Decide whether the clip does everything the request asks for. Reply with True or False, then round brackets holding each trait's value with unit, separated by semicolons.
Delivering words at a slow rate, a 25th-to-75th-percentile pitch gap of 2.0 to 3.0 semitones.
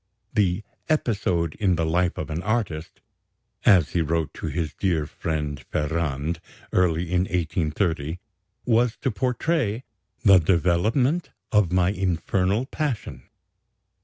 False (120 wpm; 4.6 semitones)